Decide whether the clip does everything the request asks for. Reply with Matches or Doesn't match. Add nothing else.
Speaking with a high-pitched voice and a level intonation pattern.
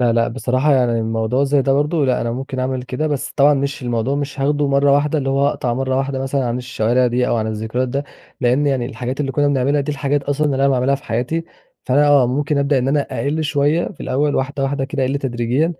Doesn't match